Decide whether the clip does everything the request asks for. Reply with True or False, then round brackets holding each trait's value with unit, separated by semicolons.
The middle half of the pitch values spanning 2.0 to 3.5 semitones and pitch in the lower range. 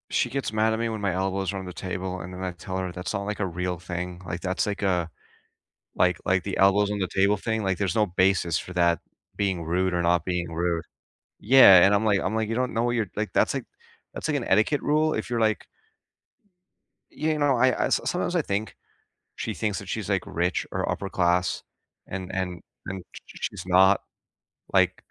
True (2.9 semitones; 95 Hz)